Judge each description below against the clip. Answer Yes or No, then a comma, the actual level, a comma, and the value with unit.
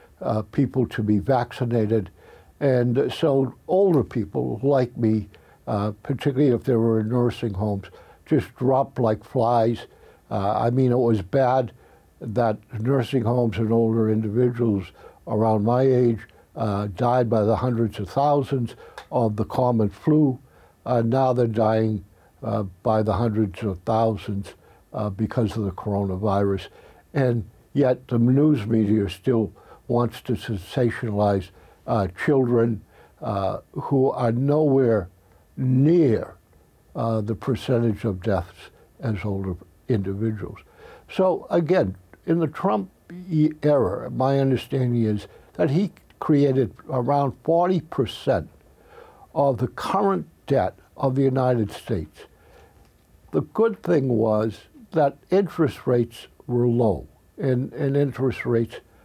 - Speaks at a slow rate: Yes, slow, 125 wpm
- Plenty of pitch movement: No, average, 3.7 semitones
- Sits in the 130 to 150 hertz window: No, low, 120 Hz